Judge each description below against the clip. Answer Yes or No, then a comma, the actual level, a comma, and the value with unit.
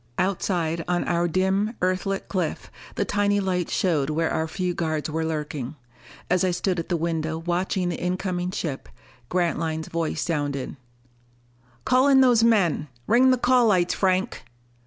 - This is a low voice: No, medium, 180 Hz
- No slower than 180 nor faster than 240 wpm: No, average, 155 wpm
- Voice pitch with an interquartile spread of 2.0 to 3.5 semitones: Yes, average, 3.2 semitones